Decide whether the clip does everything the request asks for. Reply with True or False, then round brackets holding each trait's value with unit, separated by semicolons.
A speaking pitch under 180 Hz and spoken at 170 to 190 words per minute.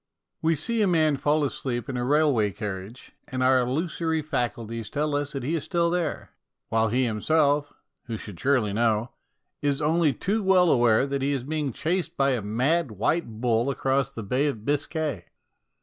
True (140 Hz; 180 wpm)